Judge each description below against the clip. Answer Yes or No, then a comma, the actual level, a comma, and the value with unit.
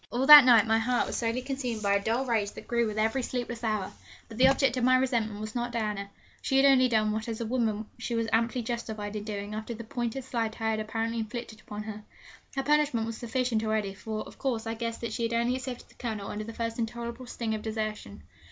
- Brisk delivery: Yes, fast, 245 wpm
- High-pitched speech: Yes, high, 230 Hz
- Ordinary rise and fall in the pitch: No, narrow, 2.1 semitones